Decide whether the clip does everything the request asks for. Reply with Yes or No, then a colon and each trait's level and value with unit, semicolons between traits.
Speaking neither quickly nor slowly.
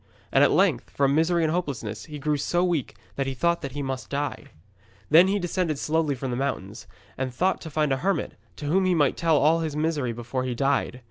No: fast, 225 wpm